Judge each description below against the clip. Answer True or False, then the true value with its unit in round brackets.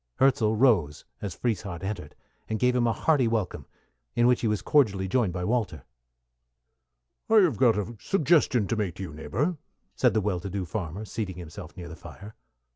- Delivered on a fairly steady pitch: False (4.9 semitones)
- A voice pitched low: True (105 Hz)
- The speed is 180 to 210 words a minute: True (190 wpm)